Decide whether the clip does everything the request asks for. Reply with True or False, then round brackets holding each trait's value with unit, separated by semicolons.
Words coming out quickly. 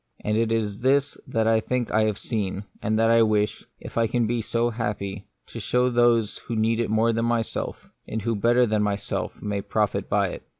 True (220 wpm)